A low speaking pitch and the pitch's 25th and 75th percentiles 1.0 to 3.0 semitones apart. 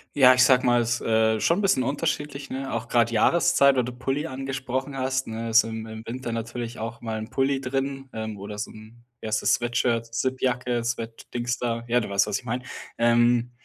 Yes: low, 120 Hz; narrow, 2.4 semitones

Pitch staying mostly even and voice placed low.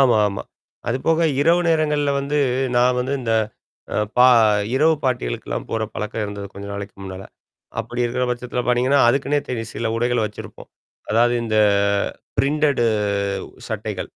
No: average, 3.8 semitones; low, 125 Hz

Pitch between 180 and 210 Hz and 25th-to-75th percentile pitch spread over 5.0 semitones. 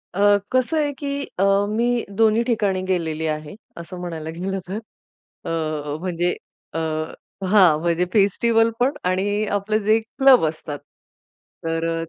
Yes: high, 195 Hz; wide, 5.4 semitones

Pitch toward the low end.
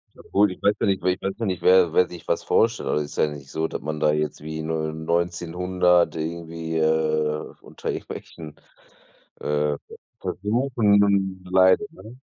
Yes: very low, 85 Hz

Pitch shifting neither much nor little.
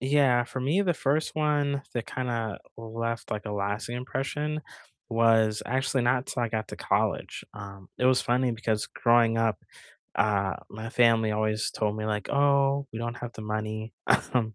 Yes: average, 3.2 semitones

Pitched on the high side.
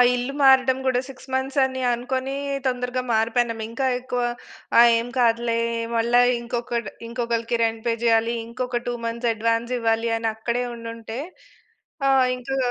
Yes: high, 240 Hz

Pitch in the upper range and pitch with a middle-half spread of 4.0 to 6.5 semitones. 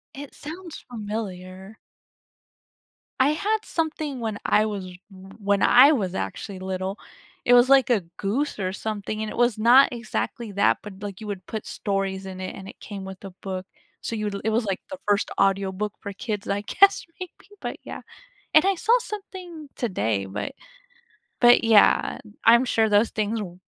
Yes: high, 210 Hz; average, 4.3 semitones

